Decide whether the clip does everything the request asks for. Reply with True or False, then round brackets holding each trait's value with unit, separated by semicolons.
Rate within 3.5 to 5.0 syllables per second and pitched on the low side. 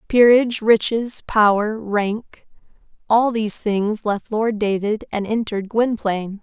False (4.1 syllables/s; 215 Hz)